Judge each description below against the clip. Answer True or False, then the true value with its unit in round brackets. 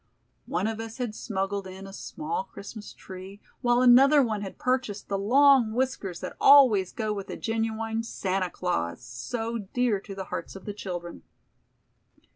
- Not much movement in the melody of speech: False (3.9 semitones)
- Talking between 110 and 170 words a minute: True (165 wpm)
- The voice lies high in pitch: True (215 Hz)